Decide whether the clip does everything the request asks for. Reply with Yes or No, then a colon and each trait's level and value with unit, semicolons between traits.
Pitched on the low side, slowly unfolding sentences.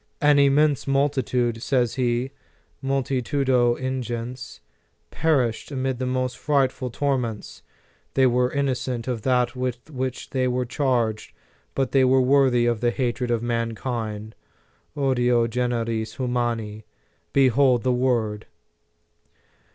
Yes: low, 125 Hz; slow, 120 wpm